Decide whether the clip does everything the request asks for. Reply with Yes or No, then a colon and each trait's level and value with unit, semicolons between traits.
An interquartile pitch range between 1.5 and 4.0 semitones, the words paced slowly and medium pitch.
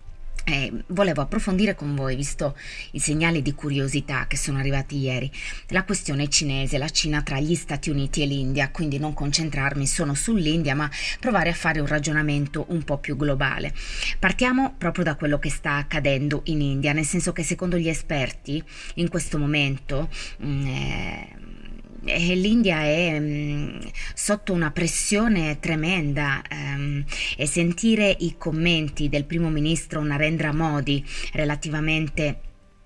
No: average, 2.9 semitones; average, 140 wpm; medium, 150 Hz